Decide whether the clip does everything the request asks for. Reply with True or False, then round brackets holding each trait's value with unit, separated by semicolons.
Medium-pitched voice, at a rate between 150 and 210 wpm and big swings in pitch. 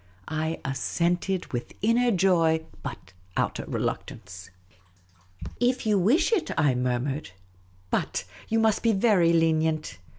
False (165 Hz; 135 wpm; 8.6 semitones)